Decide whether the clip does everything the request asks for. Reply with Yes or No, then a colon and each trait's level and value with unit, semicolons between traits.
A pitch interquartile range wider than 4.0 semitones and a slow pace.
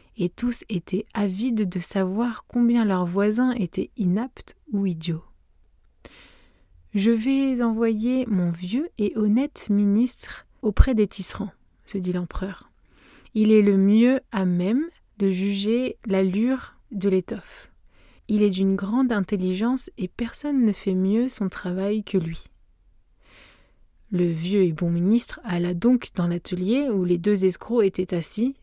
Yes: average, 4.4 semitones; slow, 140 wpm